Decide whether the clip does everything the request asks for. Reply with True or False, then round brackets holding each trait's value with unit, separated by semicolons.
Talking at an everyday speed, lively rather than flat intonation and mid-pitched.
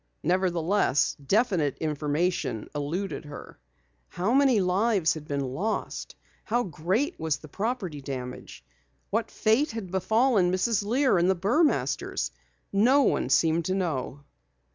False (125 wpm; 6.4 semitones; 180 Hz)